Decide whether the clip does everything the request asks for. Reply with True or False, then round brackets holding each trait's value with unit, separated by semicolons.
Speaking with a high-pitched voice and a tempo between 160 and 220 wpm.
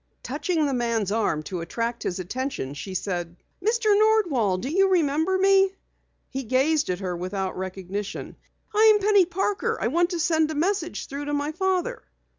True (290 Hz; 175 wpm)